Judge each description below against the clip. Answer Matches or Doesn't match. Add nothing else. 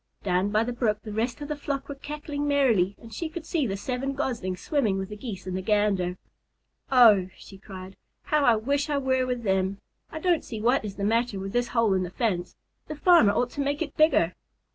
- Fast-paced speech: Matches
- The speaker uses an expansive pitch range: Matches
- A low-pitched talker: Doesn't match